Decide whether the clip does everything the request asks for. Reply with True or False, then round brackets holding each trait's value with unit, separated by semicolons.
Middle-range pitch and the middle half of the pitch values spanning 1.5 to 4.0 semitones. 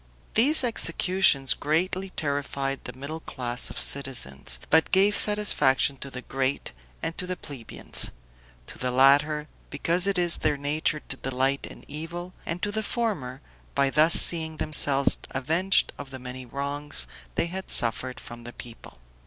False (145 Hz; 4.7 semitones)